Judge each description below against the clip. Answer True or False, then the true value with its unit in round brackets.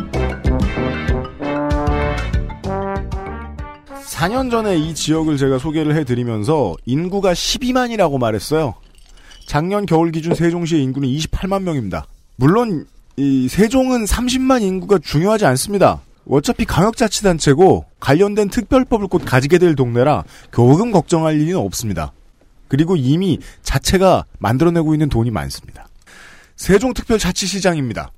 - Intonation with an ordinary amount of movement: False (8.2 semitones)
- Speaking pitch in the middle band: True (155 Hz)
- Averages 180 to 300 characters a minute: True (280 characters per minute)